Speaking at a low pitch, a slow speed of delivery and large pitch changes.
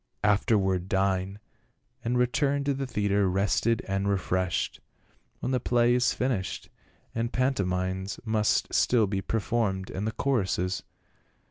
No: low, 105 Hz; slow, 125 wpm; average, 4.1 semitones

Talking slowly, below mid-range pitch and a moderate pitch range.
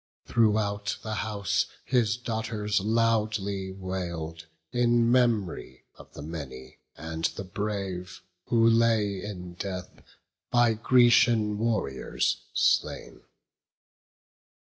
Yes: slow, 95 wpm; low, 105 Hz; average, 3.8 semitones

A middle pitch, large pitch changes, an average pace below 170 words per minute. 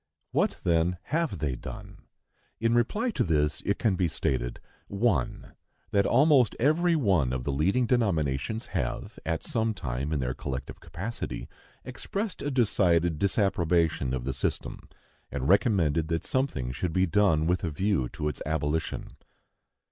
No: very low, 90 Hz; wide, 7.2 semitones; average, 150 wpm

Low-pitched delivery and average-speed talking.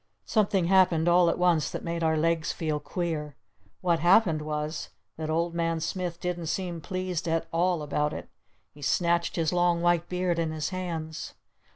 No: medium, 170 Hz; average, 175 wpm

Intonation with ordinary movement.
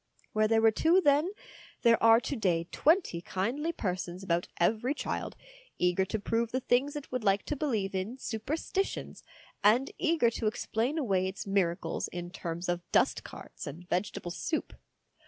No: wide, 6.4 semitones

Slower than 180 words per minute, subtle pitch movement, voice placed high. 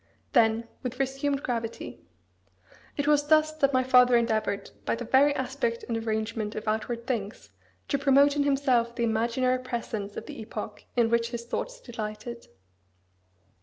No: average, 155 wpm; average, 3.1 semitones; high, 235 Hz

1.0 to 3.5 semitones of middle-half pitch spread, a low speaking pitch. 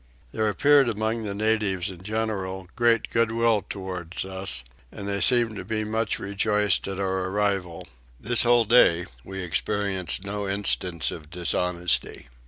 Yes: average, 2.8 semitones; low, 100 Hz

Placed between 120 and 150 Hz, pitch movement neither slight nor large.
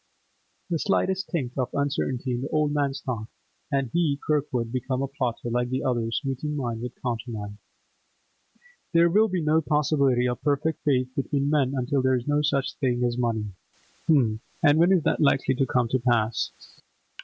Yes: low, 135 Hz; average, 3.4 semitones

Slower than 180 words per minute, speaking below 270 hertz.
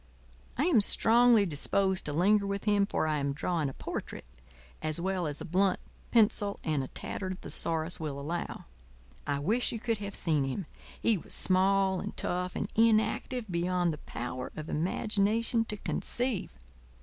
Yes: average, 165 wpm; medium, 185 Hz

